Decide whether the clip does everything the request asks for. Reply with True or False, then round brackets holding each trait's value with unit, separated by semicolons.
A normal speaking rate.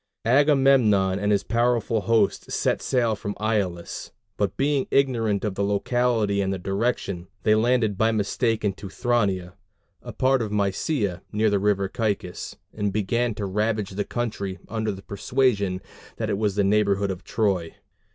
True (160 wpm)